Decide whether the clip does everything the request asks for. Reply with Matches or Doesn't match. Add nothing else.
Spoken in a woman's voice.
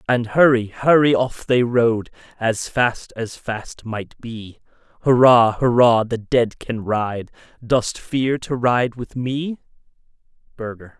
Doesn't match